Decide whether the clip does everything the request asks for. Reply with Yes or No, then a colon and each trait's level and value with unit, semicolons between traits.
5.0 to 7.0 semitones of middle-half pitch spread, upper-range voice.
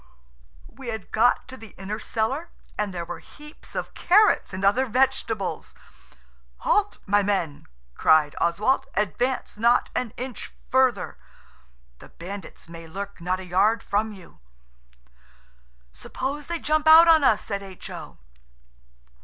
Yes: wide, 5.5 semitones; high, 215 Hz